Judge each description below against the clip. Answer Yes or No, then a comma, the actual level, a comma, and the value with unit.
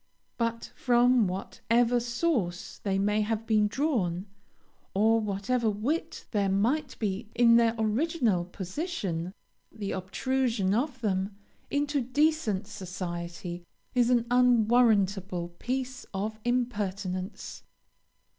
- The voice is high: Yes, high, 220 Hz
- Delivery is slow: Yes, slow, 105 wpm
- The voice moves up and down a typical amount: Yes, average, 4.3 semitones